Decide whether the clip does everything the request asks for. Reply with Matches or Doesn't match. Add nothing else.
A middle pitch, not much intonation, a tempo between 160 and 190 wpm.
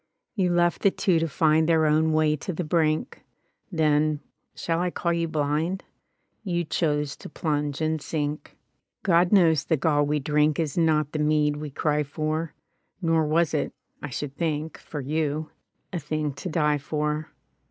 Matches